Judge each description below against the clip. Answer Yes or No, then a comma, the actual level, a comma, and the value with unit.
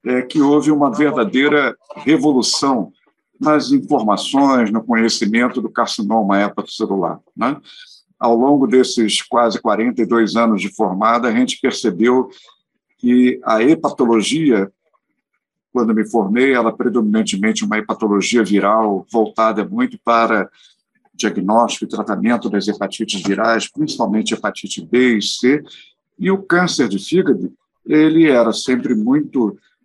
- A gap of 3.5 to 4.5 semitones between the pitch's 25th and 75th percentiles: No, average, 5.0 semitones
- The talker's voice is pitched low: Yes, low, 120 Hz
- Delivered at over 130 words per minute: No, average, 125 wpm